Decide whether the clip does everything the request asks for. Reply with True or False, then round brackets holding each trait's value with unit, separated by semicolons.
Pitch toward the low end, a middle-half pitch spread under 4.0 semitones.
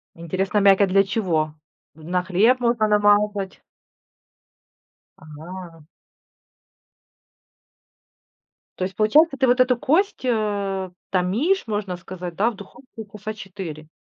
False (200 Hz; 3.5 semitones)